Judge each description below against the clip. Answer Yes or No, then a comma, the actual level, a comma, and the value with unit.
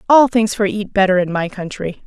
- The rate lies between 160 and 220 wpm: No, fast, 230 wpm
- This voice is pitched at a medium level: No, high, 205 Hz